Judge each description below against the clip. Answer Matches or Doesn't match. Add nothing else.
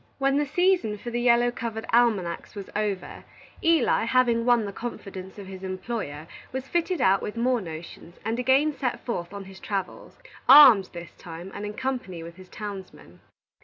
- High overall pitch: Matches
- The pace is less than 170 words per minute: Doesn't match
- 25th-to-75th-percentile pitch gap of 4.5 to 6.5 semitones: Matches